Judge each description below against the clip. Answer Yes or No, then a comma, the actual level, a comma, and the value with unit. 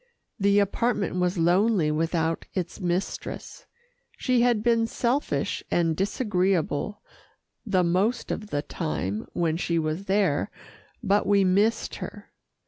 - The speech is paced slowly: Yes, slow, 125 wpm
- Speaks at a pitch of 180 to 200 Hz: Yes, high, 190 Hz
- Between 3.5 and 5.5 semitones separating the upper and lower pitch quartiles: Yes, average, 4.0 semitones